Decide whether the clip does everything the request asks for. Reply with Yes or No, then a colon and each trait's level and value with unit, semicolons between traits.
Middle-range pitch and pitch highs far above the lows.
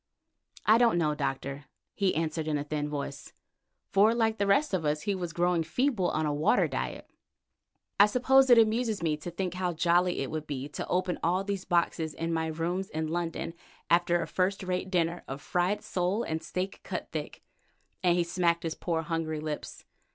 No: medium, 175 Hz; average, 3.3 semitones